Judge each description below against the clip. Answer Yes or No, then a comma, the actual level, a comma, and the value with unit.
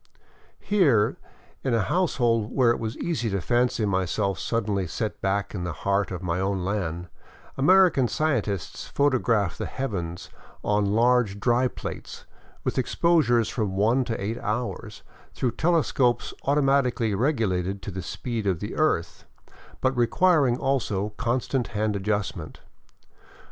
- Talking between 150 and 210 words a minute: No, average, 140 wpm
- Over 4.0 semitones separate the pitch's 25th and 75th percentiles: Yes, average, 4.7 semitones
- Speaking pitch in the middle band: No, low, 115 Hz